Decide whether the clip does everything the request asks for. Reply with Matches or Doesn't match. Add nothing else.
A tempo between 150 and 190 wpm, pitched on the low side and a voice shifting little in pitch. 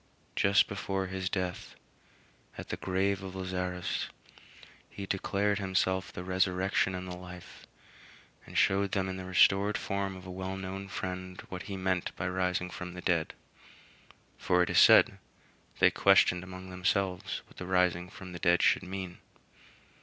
Matches